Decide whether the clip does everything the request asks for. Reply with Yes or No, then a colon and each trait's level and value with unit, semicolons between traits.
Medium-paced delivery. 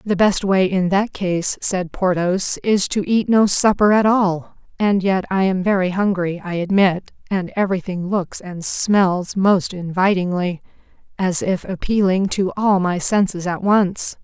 Yes: average, 165 wpm